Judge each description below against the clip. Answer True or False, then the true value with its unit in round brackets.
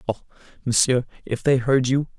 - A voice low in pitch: True (125 Hz)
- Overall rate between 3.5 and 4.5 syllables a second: False (5.2 syllables/s)